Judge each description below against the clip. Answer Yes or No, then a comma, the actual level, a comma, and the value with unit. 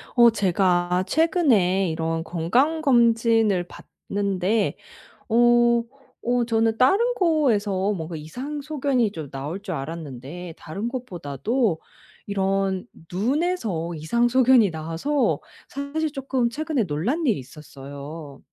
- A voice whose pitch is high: Yes, high, 205 Hz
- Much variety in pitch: Yes, wide, 7.1 semitones